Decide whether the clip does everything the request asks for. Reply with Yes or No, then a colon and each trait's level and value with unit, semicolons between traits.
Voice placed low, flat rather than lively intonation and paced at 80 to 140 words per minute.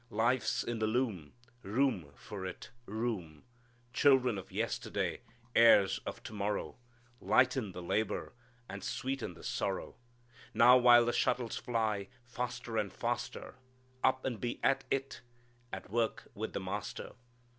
No: low, 115 Hz; average, 3.8 semitones; slow, 135 wpm